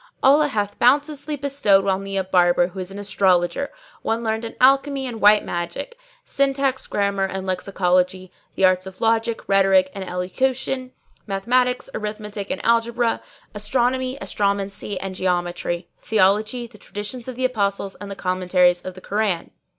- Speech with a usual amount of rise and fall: Yes, average, 4.8 semitones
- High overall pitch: Yes, high, 205 Hz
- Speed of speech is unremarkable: Yes, average, 150 wpm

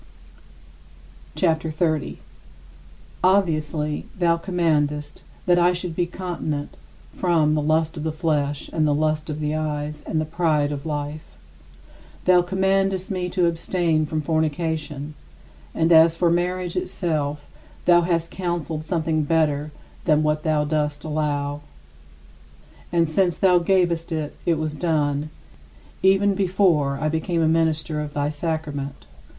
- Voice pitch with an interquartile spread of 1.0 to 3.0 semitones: Yes, narrow, 2.5 semitones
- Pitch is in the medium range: Yes, medium, 160 Hz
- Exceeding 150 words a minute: No, slow, 135 wpm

